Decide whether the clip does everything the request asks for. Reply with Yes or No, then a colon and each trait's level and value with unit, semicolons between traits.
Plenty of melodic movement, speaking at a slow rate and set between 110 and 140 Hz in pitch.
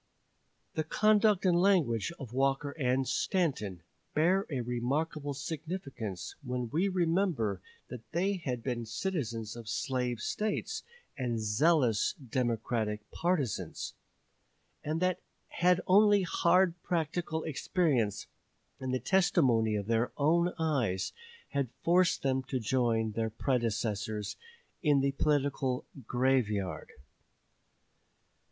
Yes: wide, 6.5 semitones; slow, 110 wpm; low, 135 Hz